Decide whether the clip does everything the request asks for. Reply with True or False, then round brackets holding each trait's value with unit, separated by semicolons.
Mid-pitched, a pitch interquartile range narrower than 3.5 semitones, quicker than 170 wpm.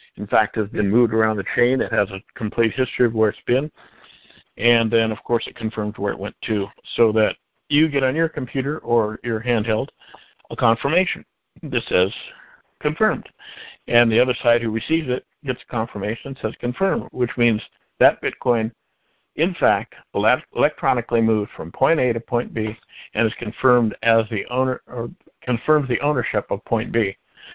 False (120 Hz; 2.7 semitones; 180 wpm)